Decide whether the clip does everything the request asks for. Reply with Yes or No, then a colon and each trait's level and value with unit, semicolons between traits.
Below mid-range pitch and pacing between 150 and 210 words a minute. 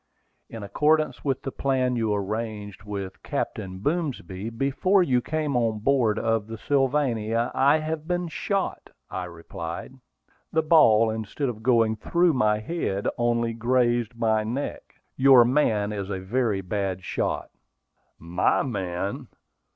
No: low, 115 Hz; slow, 135 wpm